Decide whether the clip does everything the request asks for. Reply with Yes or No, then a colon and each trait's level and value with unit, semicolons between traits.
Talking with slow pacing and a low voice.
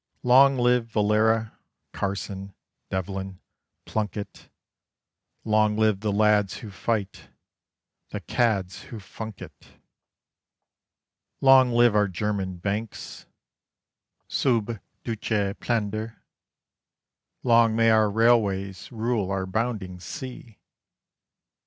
Yes: slow, 90 wpm; low, 110 Hz